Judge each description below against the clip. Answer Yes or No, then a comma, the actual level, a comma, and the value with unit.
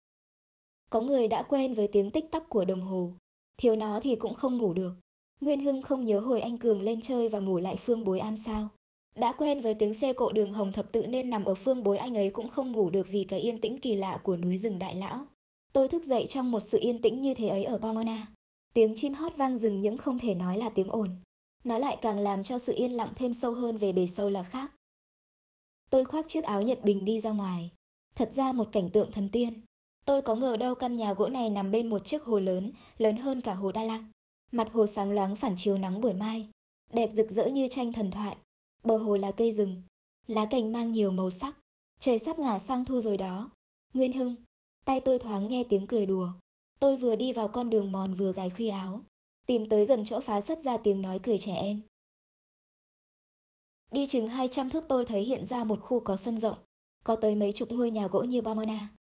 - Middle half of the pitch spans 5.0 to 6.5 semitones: No, average, 3.5 semitones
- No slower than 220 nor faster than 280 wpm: Yes, average, 235 wpm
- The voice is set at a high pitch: Yes, high, 225 Hz